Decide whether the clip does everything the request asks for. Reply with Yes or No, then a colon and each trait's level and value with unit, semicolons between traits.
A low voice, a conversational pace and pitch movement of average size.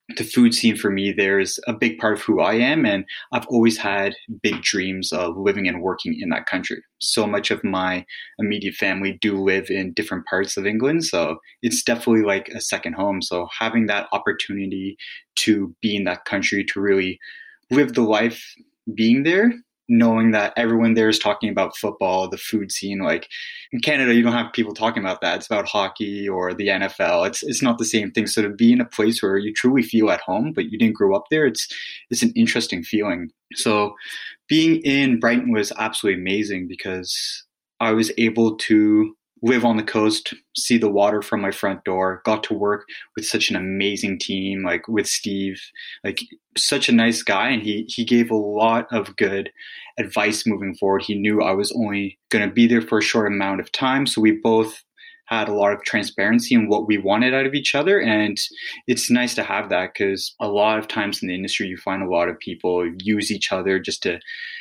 No: low, 110 Hz; fast, 210 wpm; average, 3.1 semitones